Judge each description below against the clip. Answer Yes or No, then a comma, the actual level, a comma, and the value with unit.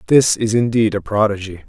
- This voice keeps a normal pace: Yes, average, 180 wpm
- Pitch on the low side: Yes, low, 110 Hz